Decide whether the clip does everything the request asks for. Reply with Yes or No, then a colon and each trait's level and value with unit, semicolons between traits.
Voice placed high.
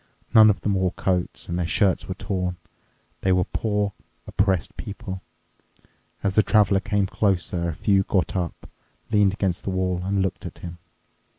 No: very low, 95 Hz